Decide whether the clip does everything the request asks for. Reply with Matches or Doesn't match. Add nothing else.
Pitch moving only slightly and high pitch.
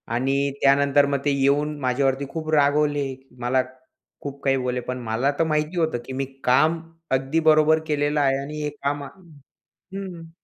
Doesn't match